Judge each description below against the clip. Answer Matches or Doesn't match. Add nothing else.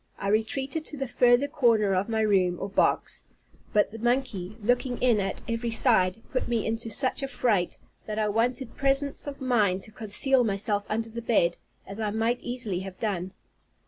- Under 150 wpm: Doesn't match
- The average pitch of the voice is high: Matches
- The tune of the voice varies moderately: Matches